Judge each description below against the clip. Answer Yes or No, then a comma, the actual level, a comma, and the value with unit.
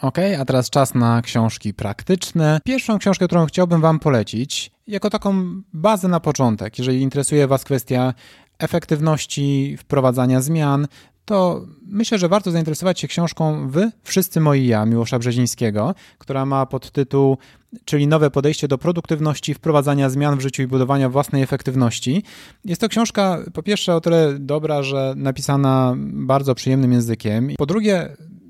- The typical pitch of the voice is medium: Yes, medium, 145 Hz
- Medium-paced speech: Yes, average, 145 wpm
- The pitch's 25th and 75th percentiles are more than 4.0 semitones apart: Yes, average, 4.6 semitones